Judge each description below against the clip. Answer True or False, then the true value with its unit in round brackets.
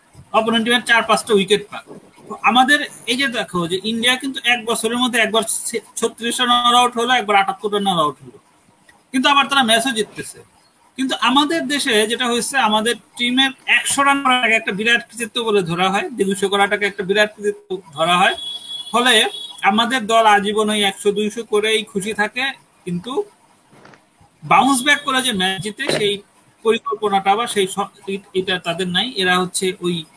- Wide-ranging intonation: False (3.7 semitones)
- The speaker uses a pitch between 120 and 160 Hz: False (225 Hz)